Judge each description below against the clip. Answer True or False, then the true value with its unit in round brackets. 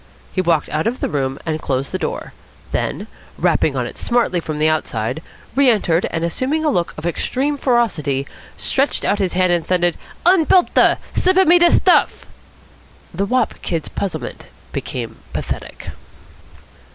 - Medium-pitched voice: True (180 Hz)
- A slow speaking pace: False (165 wpm)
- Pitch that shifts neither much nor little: False (8.6 semitones)